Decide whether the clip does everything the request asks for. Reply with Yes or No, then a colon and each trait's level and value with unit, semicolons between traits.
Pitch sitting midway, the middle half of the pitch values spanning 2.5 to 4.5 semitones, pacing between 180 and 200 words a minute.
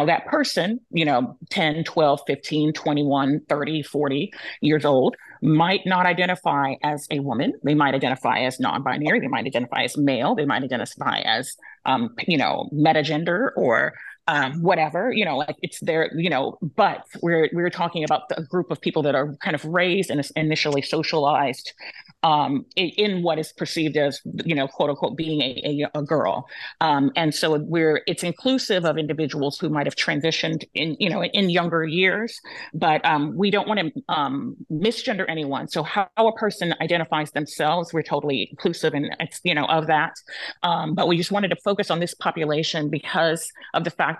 Yes: medium, 160 Hz; average, 3.0 semitones; average, 185 wpm